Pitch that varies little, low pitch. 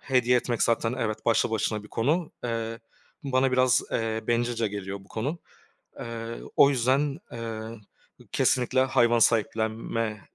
Yes: narrow, 2.2 semitones; low, 115 Hz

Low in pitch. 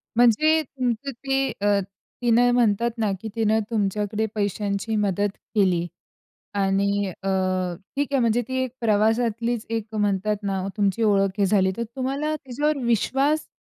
No: high, 220 Hz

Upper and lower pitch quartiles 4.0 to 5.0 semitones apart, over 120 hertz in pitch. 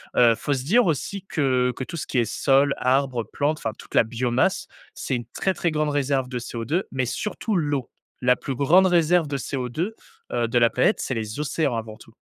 Yes: average, 4.3 semitones; low, 135 Hz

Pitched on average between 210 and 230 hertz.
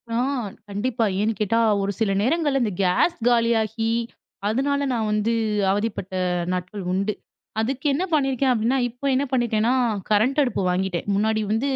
Yes: high, 225 Hz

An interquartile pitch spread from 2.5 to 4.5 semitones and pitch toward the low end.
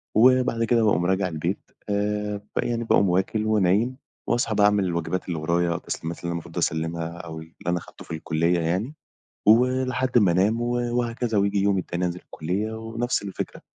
No: average, 5.0 semitones; low, 100 Hz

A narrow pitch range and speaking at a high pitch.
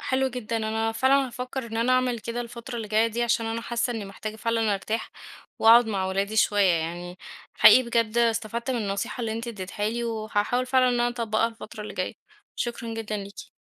Yes: narrow, 1.9 semitones; high, 225 Hz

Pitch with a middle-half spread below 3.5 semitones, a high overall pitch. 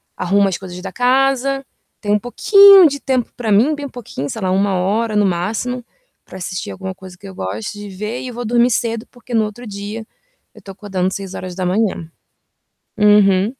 No: average, 4.4 semitones; high, 210 Hz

